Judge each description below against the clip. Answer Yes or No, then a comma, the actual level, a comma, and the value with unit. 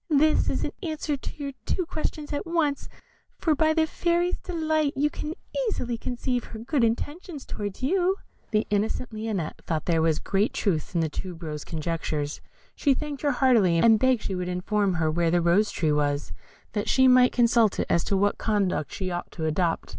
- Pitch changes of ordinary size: No, wide, 8.9 semitones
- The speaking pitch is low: No, high, 225 Hz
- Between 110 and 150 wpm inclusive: No, average, 195 wpm